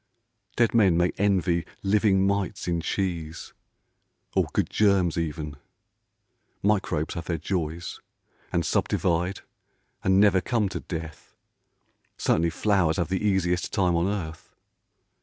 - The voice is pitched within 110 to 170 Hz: No, very low, 90 Hz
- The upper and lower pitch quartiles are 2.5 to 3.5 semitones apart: Yes, average, 2.9 semitones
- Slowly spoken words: Yes, slow, 120 wpm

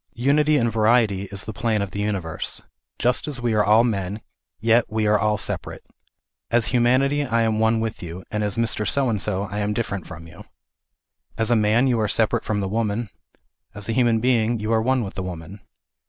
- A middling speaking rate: No, fast, 215 wpm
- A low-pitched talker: Yes, low, 110 Hz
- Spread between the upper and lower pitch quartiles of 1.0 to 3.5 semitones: Yes, narrow, 2.4 semitones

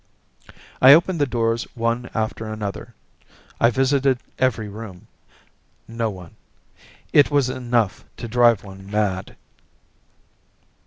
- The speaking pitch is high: No, low, 115 Hz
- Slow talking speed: Yes, slow, 110 wpm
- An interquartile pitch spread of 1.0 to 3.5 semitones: Yes, average, 3.2 semitones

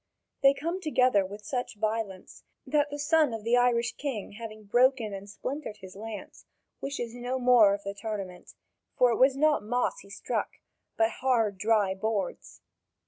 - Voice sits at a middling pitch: No, high, 230 Hz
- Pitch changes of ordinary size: Yes, average, 4.1 semitones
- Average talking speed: Yes, average, 165 wpm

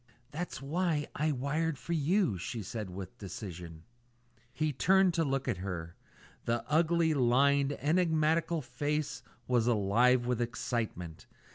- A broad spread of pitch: Yes, wide, 5.8 semitones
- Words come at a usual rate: No, slow, 130 wpm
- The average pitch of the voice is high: No, low, 135 Hz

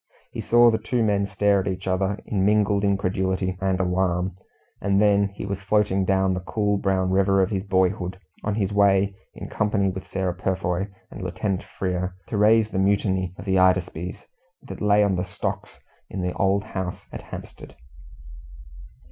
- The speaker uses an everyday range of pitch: No, narrow, 1.5 semitones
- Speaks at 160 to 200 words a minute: Yes, average, 175 wpm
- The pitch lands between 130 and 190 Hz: No, very low, 95 Hz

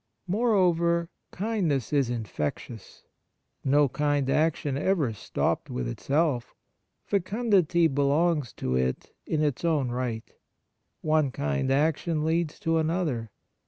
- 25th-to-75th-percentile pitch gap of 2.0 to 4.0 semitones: No, average, 4.8 semitones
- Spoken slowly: Yes, slow, 110 wpm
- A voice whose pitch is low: No, medium, 150 Hz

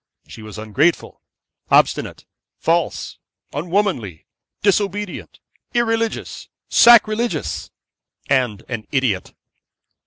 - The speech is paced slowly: Yes, slow, 70 wpm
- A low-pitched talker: No, medium, 170 Hz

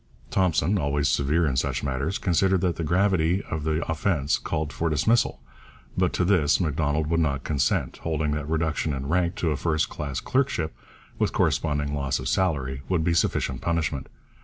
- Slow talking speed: No, average, 175 wpm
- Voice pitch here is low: Yes, very low, 80 Hz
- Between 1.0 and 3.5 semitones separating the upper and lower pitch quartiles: Yes, average, 3.2 semitones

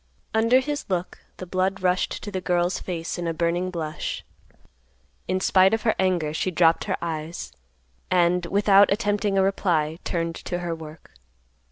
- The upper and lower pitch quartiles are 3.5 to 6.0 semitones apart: No, narrow, 2.6 semitones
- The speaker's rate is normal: Yes, average, 165 wpm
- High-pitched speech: No, medium, 180 Hz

